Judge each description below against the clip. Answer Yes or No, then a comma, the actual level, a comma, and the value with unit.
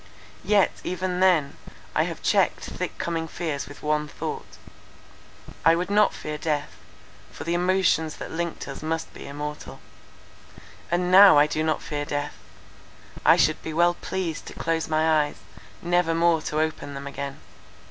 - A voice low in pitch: No, medium, 160 Hz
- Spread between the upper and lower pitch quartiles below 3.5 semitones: Yes, average, 2.7 semitones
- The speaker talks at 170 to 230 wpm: No, average, 160 wpm